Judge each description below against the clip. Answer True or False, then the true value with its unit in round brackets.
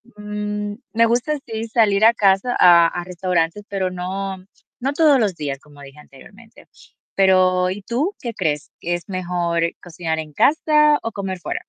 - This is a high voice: True (195 Hz)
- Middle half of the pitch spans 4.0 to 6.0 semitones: True (4.3 semitones)